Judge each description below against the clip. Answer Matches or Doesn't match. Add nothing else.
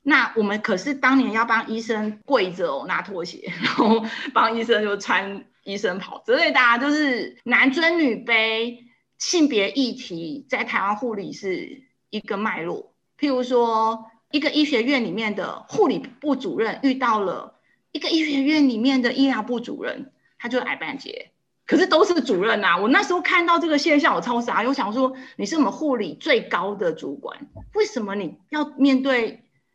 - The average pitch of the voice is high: Matches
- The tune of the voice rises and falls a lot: Doesn't match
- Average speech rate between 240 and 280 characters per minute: Matches